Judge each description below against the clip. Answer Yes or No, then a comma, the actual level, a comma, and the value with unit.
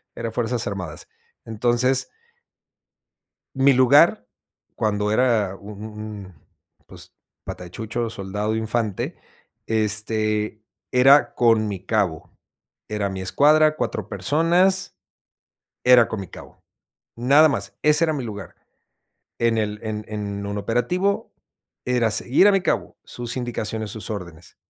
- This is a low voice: Yes, low, 110 Hz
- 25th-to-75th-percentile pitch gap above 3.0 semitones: Yes, average, 3.5 semitones